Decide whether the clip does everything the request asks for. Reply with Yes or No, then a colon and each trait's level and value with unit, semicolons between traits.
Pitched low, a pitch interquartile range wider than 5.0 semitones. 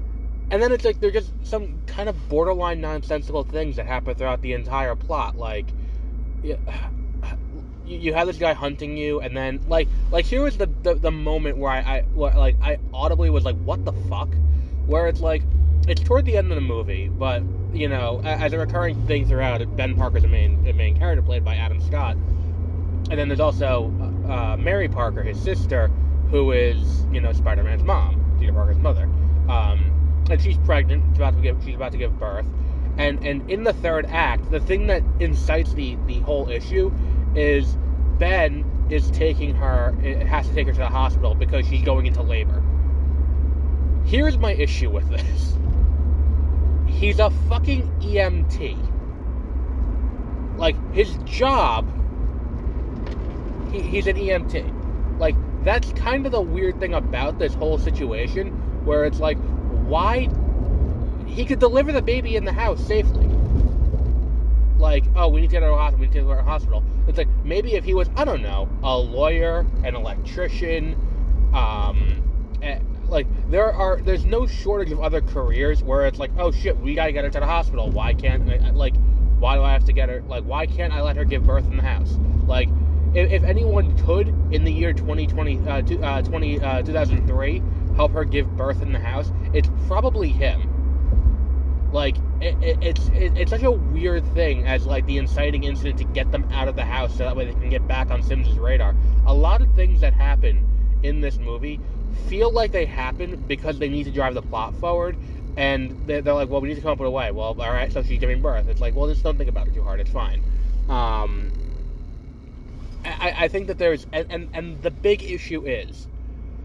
Yes: very low, 75 Hz; wide, 5.4 semitones